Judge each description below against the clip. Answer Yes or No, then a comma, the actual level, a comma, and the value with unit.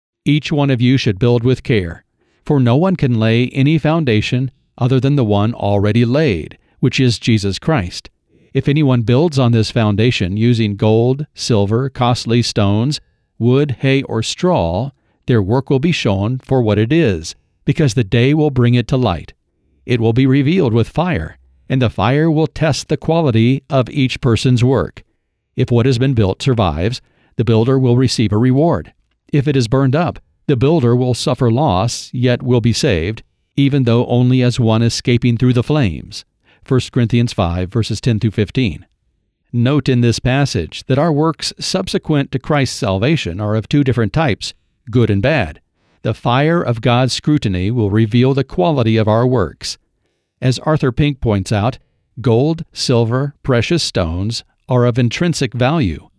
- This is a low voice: Yes, low, 125 Hz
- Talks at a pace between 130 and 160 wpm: No, average, 170 wpm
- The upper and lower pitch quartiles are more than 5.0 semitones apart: No, average, 3.8 semitones